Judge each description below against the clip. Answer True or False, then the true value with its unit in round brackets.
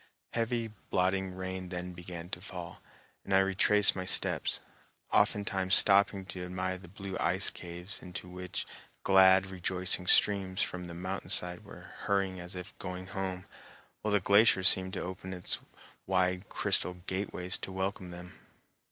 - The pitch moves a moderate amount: False (1.2 semitones)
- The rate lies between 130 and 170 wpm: True (150 wpm)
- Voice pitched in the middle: False (95 Hz)